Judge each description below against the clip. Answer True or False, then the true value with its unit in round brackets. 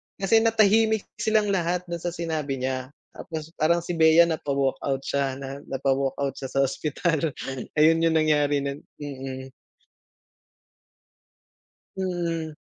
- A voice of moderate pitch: True (155 Hz)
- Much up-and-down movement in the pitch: False (3.8 semitones)